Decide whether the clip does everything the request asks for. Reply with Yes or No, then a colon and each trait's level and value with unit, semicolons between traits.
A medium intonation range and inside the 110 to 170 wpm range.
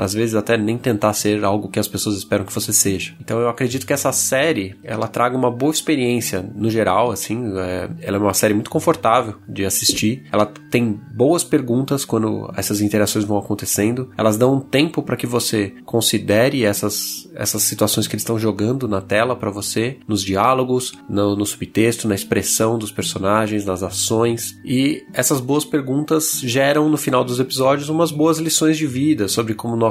No: average, 4.0 semitones; fast, 185 wpm